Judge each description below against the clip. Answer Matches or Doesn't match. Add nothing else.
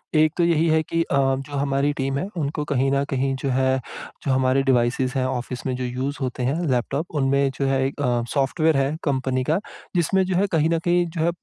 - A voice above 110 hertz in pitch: Matches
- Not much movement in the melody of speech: Doesn't match